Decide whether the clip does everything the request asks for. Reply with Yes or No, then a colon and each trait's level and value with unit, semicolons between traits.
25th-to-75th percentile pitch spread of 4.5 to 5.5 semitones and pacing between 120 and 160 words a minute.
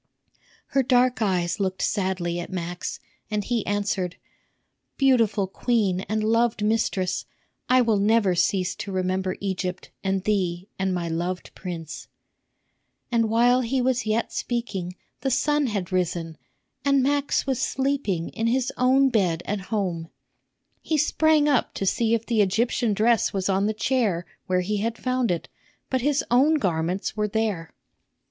Yes: average, 4.9 semitones; average, 155 wpm